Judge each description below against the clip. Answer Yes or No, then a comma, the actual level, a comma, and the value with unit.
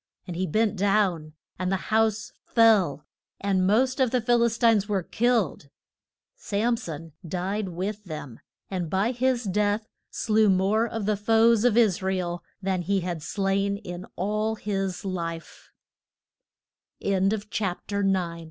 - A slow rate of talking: Yes, slow, 125 wpm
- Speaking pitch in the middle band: No, high, 205 Hz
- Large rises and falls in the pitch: No, average, 3.3 semitones